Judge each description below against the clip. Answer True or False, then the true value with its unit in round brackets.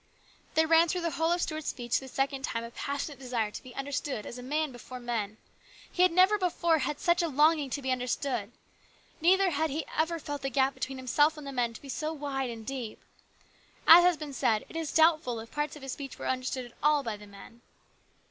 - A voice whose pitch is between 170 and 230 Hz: False (280 Hz)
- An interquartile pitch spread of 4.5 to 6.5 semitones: False (4.1 semitones)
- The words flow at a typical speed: False (230 wpm)